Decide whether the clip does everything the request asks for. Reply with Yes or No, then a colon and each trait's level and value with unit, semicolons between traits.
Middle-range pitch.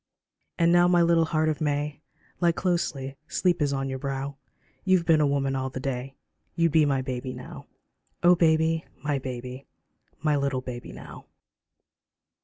Yes: medium, 145 Hz